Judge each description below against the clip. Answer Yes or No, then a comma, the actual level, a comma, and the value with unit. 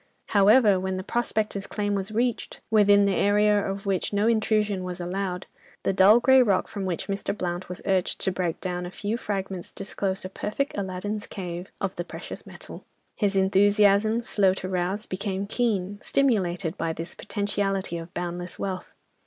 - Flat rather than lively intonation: Yes, narrow, 2.0 semitones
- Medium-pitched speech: No, high, 195 Hz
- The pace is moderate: Yes, average, 170 wpm